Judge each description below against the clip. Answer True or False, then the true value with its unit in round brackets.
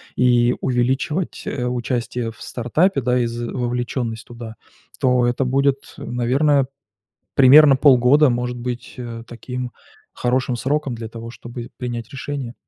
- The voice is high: False (125 Hz)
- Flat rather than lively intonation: True (1.8 semitones)